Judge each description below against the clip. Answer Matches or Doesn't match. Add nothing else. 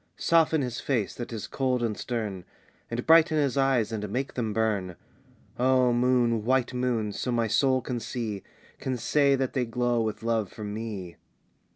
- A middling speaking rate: Matches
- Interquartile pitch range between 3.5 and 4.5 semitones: Doesn't match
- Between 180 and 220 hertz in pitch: Doesn't match